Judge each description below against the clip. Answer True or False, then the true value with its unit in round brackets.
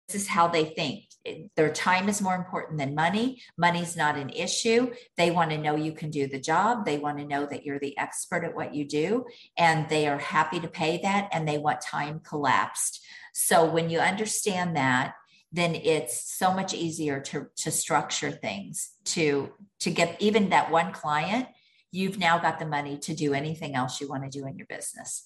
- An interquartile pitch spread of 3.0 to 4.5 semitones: True (3.9 semitones)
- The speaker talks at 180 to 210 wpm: True (205 wpm)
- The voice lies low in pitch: False (165 Hz)